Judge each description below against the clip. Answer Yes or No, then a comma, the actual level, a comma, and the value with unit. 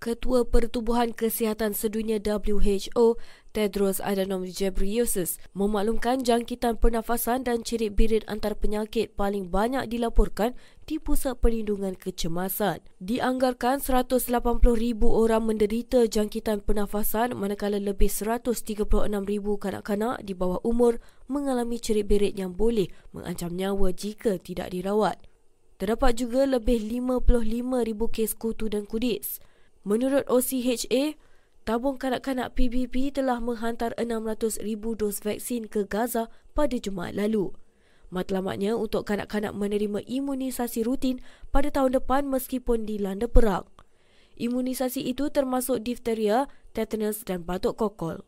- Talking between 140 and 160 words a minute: No, average, 110 wpm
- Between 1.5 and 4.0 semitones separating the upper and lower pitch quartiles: Yes, average, 2.9 semitones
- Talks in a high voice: Yes, high, 225 Hz